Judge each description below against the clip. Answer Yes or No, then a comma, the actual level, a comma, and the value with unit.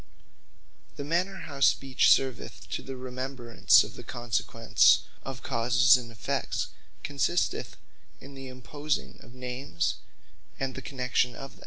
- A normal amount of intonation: No, narrow, 2.0 semitones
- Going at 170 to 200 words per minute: No, slow, 135 wpm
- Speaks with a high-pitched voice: No, low, 130 Hz